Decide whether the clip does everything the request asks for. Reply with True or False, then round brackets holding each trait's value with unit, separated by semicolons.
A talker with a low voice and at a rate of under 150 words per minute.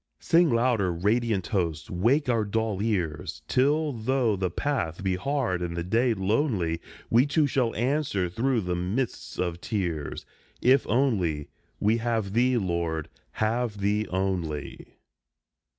True (105 Hz; 135 wpm)